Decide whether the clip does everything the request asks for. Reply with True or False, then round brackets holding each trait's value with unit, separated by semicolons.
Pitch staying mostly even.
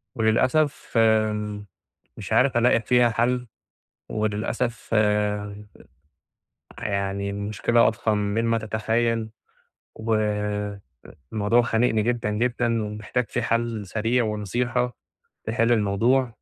True (2.1 semitones)